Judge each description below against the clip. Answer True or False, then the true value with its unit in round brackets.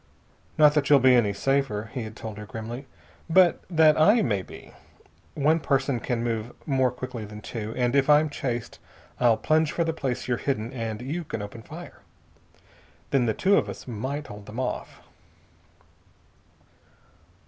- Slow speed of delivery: False (170 wpm)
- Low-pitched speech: True (125 Hz)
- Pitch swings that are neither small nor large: True (4.6 semitones)